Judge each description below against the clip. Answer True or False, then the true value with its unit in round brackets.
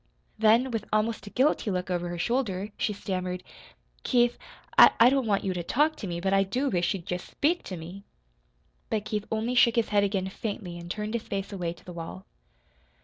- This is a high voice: True (200 Hz)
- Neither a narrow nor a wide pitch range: True (4.1 semitones)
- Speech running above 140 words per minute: True (205 wpm)